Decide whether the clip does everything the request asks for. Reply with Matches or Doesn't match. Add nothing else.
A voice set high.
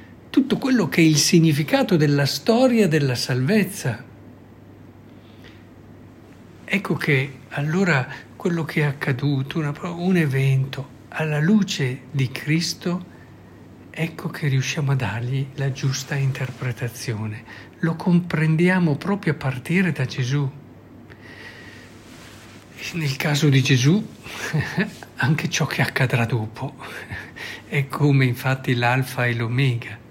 Doesn't match